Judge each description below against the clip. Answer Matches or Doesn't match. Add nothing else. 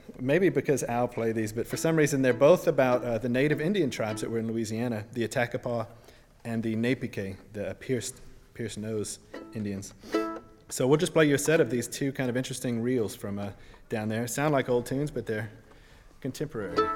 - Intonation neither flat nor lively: Matches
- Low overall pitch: Matches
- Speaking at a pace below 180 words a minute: Doesn't match